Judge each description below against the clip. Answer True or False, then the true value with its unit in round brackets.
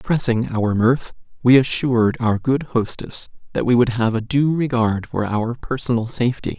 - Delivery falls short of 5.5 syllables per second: True (5.0 syllables/s)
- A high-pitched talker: False (120 Hz)